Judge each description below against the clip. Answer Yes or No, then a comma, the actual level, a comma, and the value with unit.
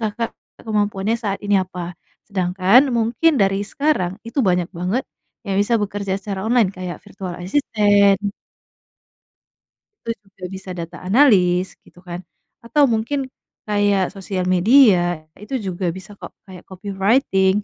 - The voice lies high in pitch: Yes, high, 200 Hz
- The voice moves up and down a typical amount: Yes, average, 3.3 semitones